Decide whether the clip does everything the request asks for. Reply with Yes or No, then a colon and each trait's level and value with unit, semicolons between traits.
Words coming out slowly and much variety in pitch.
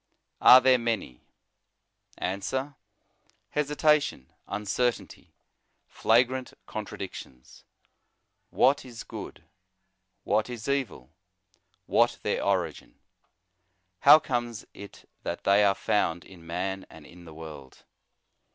Yes: slow, 95 wpm; wide, 6.3 semitones